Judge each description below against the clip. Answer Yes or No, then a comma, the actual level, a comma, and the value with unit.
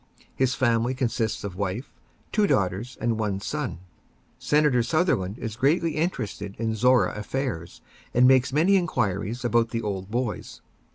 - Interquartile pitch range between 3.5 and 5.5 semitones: Yes, average, 4.2 semitones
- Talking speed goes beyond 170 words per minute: No, average, 145 wpm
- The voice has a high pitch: No, low, 120 Hz